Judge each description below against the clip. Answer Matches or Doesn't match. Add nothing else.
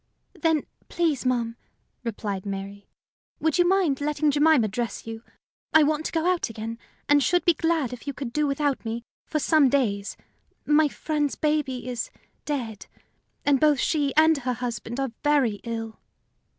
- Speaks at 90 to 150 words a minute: Doesn't match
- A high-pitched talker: Matches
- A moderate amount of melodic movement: Matches